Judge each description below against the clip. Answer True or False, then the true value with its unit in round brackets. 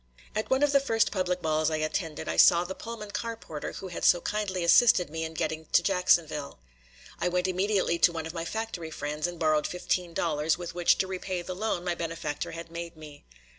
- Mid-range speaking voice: True (175 Hz)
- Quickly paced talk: True (215 wpm)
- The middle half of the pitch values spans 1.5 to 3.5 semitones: True (2.9 semitones)